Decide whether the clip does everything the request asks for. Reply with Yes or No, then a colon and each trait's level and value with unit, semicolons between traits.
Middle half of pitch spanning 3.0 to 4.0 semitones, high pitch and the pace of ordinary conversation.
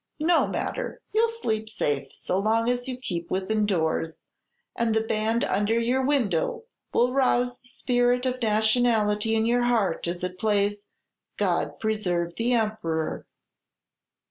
Yes: average, 3.4 semitones; high, 220 Hz; average, 145 wpm